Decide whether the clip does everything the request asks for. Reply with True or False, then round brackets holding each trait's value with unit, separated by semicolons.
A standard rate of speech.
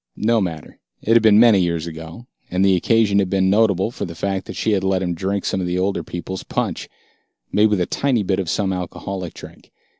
False (230 wpm)